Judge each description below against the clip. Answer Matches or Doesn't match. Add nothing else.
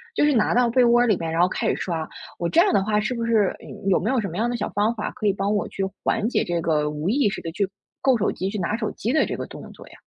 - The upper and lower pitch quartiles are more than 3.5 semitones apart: Matches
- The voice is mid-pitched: Doesn't match